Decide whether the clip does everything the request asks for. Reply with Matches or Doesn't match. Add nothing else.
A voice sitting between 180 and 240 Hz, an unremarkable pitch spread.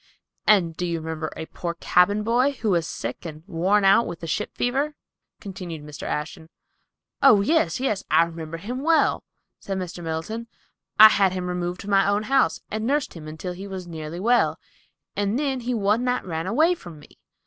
Doesn't match